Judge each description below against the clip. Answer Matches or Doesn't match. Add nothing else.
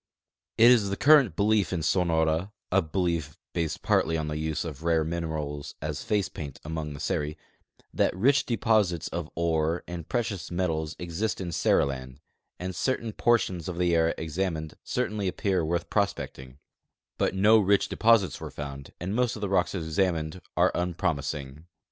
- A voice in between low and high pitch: Doesn't match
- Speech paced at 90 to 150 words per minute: Doesn't match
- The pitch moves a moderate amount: Matches